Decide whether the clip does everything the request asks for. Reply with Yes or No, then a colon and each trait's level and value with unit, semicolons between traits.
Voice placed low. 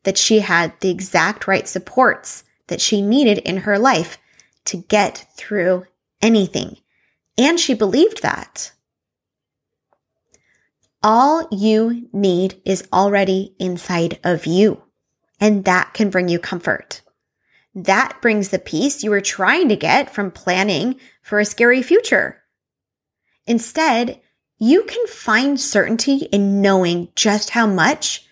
No: high, 205 Hz